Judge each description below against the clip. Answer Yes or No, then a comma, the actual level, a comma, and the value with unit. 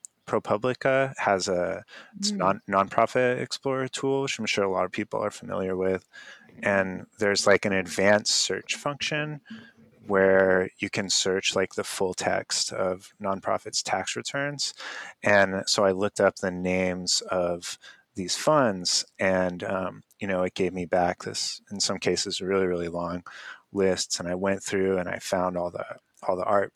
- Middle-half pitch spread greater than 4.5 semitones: No, average, 3.7 semitones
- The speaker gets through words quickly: No, average, 170 wpm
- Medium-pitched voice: No, very low, 95 Hz